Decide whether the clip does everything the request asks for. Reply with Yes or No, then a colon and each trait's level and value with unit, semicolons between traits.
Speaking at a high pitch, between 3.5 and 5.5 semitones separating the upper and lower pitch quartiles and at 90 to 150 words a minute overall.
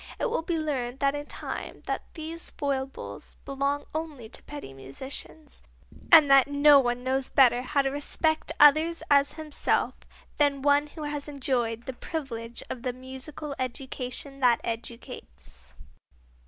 No: very high, 275 Hz; average, 2.9 semitones; average, 140 wpm